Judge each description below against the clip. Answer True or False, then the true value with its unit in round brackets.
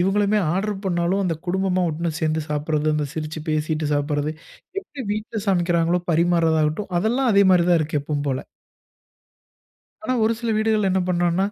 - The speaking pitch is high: False (175 Hz)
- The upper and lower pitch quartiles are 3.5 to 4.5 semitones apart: True (4.2 semitones)